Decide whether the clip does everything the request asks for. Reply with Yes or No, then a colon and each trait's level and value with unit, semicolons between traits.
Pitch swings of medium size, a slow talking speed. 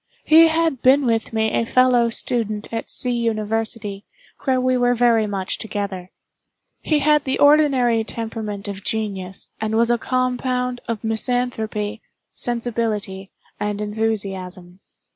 Yes: average, 3.1 semitones; slow, 130 wpm